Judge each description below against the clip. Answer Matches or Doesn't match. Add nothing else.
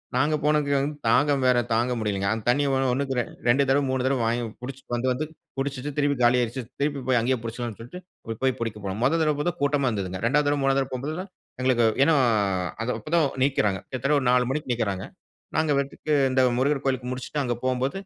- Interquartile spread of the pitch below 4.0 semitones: Matches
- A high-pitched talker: Doesn't match